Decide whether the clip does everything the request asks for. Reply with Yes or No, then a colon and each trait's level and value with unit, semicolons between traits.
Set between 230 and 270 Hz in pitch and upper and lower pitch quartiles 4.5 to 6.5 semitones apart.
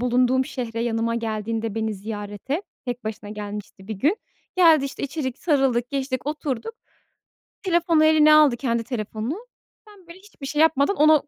Yes: very high, 260 Hz; average, 5.3 semitones